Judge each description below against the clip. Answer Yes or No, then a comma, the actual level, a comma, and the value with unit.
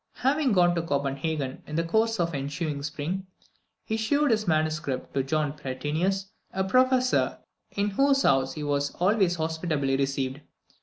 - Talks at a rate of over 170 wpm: No, average, 155 wpm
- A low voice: No, medium, 160 Hz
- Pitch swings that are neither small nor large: No, wide, 5.9 semitones